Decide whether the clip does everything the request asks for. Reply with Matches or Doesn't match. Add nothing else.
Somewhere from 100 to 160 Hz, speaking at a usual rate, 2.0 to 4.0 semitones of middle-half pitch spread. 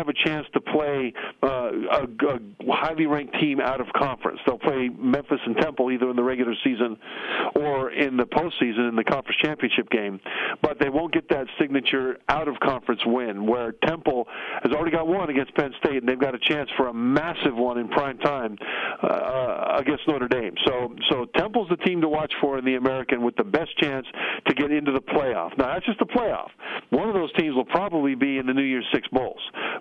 Doesn't match